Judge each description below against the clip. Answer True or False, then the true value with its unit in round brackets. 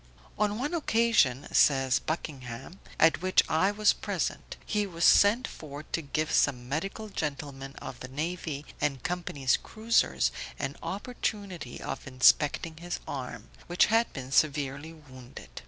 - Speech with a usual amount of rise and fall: False (6.2 semitones)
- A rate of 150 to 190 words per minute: False (140 wpm)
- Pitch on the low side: False (155 Hz)